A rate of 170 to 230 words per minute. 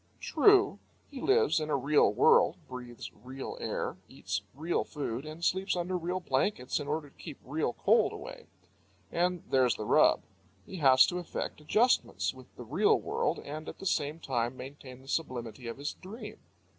Yes: average, 175 wpm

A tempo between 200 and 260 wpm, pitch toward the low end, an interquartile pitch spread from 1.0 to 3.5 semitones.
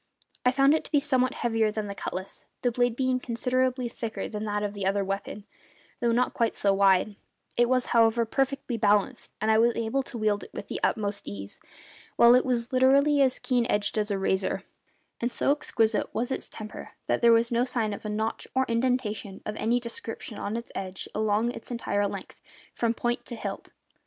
No: fast, 205 wpm; high, 230 Hz; average, 3.1 semitones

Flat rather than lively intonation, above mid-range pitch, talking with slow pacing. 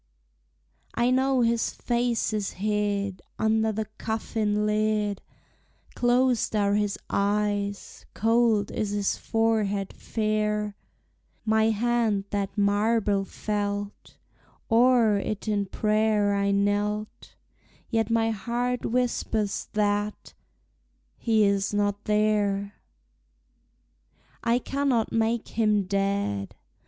Yes: narrow, 1.8 semitones; high, 210 Hz; slow, 100 wpm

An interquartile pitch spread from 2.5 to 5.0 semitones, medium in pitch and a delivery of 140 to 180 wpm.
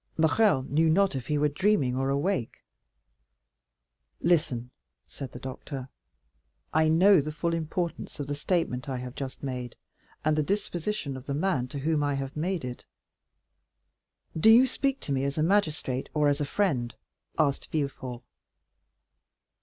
Yes: average, 4.1 semitones; medium, 150 Hz; average, 155 wpm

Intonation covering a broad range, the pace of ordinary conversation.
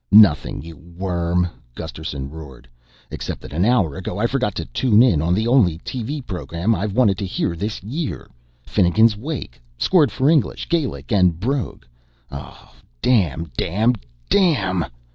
Yes: wide, 6.6 semitones; average, 150 wpm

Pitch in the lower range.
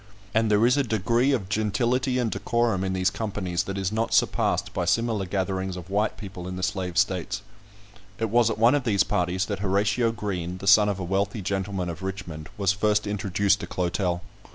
Yes: low, 100 Hz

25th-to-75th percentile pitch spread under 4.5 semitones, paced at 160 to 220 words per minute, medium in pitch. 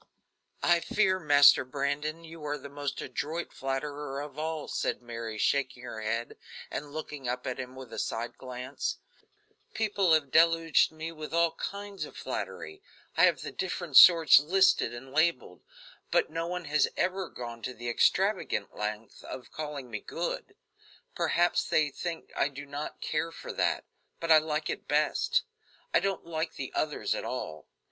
Yes: average, 4.1 semitones; average, 170 wpm; medium, 150 Hz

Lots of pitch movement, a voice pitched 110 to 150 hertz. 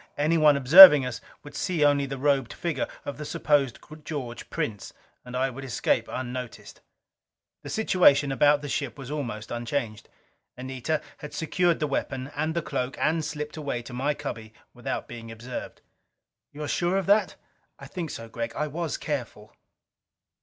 No: average, 3.4 semitones; medium, 140 Hz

